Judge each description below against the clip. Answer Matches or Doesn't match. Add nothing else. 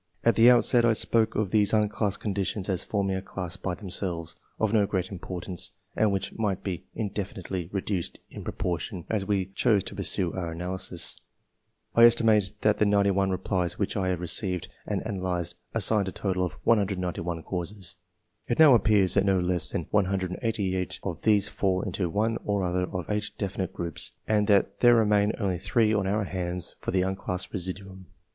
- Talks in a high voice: Doesn't match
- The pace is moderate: Matches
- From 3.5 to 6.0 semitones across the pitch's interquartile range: Doesn't match